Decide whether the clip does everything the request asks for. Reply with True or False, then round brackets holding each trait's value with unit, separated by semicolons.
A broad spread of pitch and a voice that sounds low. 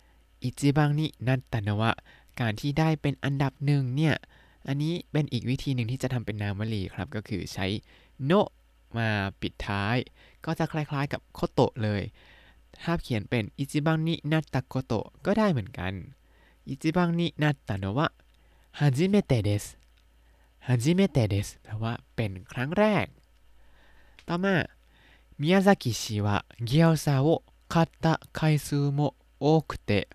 True (6.6 semitones; 130 Hz)